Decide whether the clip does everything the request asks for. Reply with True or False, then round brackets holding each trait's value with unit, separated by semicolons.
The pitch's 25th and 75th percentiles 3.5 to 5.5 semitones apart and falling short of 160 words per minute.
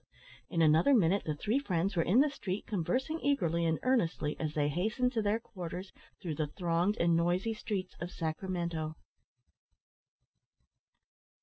True (4.8 semitones; 145 wpm)